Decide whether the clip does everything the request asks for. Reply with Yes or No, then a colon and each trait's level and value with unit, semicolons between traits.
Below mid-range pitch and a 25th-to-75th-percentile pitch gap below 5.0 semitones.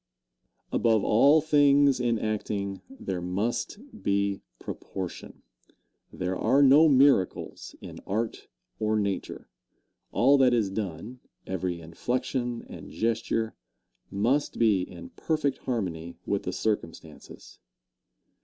No: low, 110 Hz; average, 5.3 semitones